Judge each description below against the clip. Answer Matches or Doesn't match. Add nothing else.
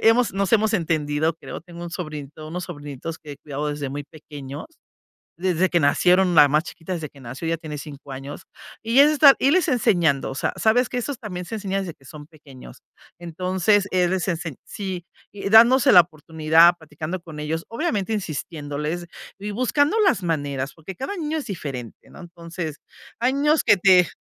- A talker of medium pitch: Matches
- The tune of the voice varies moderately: Matches